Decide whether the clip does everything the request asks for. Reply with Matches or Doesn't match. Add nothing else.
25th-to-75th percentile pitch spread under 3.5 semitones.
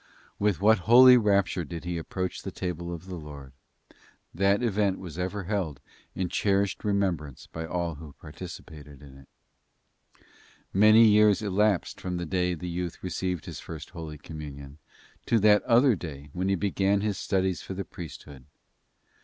Doesn't match